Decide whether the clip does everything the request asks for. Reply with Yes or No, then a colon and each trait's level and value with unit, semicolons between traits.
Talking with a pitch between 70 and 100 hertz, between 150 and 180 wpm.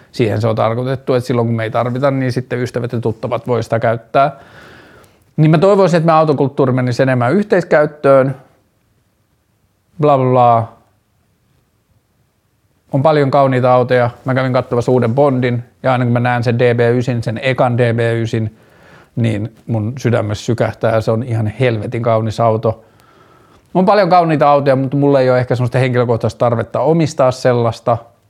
No: low, 120 Hz; fast, 155 wpm